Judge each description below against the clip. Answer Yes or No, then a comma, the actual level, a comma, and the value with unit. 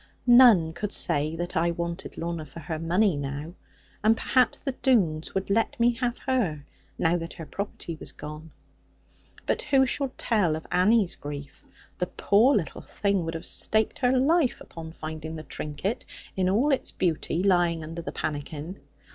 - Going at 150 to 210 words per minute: Yes, average, 170 wpm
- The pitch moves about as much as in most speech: No, wide, 5.8 semitones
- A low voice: No, medium, 175 Hz